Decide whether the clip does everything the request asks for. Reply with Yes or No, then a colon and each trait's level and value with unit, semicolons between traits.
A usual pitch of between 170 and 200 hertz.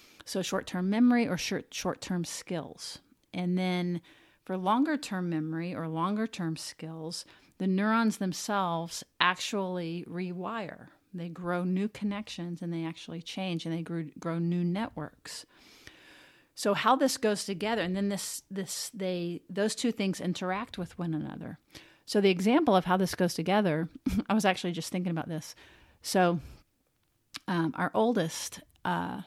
Yes: medium, 185 Hz